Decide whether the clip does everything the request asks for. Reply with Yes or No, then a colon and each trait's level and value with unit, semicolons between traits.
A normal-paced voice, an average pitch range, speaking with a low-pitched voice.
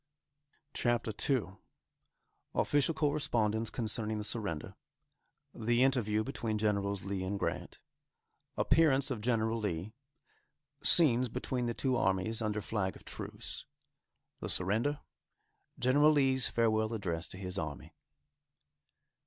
No: slow, 110 wpm; average, 4.0 semitones; low, 110 Hz